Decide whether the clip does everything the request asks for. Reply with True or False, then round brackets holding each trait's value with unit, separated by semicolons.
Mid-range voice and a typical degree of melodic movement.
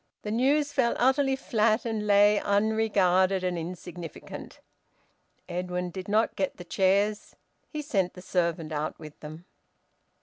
False (195 Hz; 3.8 semitones)